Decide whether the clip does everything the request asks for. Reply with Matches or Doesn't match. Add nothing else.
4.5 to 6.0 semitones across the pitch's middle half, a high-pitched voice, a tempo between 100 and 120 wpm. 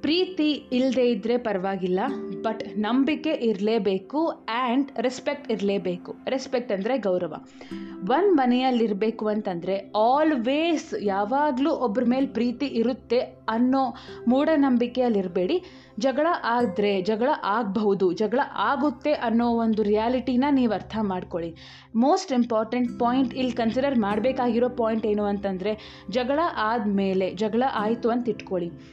Doesn't match